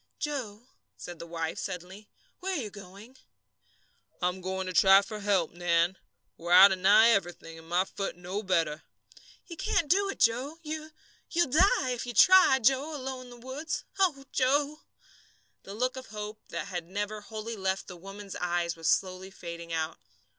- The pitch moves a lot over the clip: Yes, wide, 6.5 semitones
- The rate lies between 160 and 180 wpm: Yes, average, 175 wpm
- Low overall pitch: No, high, 205 Hz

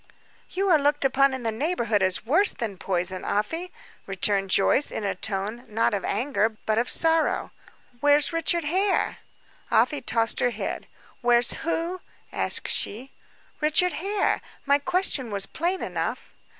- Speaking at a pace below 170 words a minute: Yes, average, 150 wpm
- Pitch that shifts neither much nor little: No, wide, 7.2 semitones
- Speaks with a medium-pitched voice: No, very high, 260 Hz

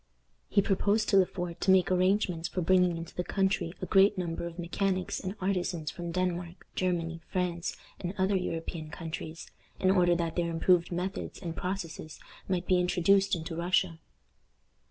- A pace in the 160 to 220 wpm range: Yes, average, 165 wpm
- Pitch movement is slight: Yes, narrow, 2.0 semitones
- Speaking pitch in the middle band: Yes, medium, 180 Hz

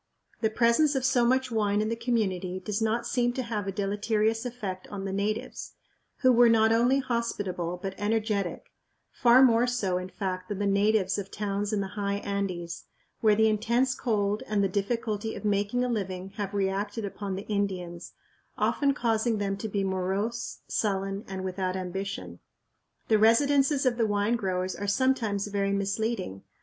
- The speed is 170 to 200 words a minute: Yes, average, 175 wpm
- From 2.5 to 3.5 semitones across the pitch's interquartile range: Yes, average, 3.0 semitones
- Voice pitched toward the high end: Yes, high, 205 Hz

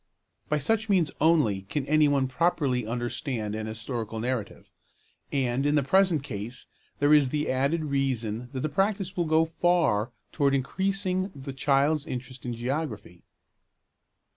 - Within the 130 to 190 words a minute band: Yes, average, 145 wpm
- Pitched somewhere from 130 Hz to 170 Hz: Yes, medium, 140 Hz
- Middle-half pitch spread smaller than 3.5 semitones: No, average, 4.6 semitones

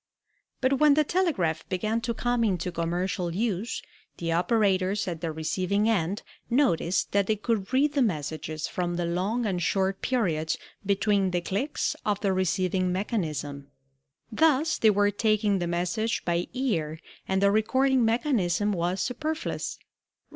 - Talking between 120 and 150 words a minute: Yes, average, 145 wpm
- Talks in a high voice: Yes, high, 200 Hz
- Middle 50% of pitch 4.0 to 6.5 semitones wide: Yes, average, 4.8 semitones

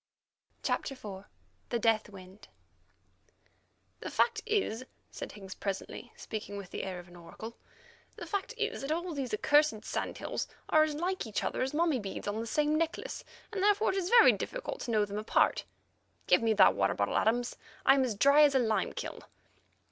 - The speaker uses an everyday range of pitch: No, wide, 7.4 semitones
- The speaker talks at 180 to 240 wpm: Yes, average, 190 wpm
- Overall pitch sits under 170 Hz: No, high, 245 Hz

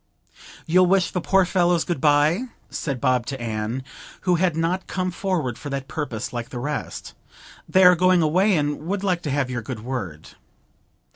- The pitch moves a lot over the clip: Yes, wide, 6.0 semitones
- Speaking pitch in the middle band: Yes, medium, 155 Hz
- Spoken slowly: No, average, 185 wpm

